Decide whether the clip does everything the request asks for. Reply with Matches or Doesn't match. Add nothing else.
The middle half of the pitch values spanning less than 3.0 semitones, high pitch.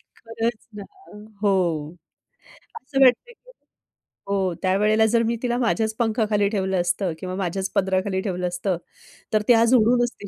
Doesn't match